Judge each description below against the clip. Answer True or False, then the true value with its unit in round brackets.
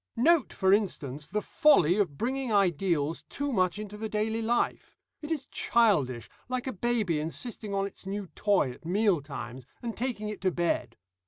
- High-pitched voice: True (205 Hz)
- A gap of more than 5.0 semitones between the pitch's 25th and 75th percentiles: True (5.6 semitones)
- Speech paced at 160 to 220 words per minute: True (175 wpm)